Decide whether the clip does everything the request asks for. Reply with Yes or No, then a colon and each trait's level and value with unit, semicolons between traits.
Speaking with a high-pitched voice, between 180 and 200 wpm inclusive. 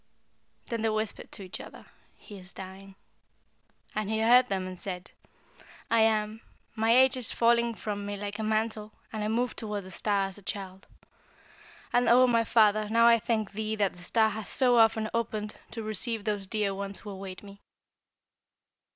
Yes: high, 215 Hz; average, 185 wpm